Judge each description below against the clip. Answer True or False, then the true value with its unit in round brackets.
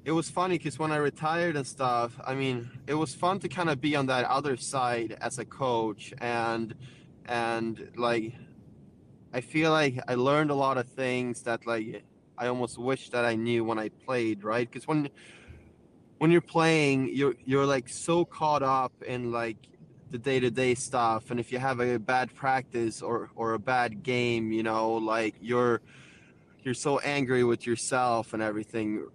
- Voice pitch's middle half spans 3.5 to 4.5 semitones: False (3.1 semitones)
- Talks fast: False (180 wpm)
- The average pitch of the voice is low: True (125 Hz)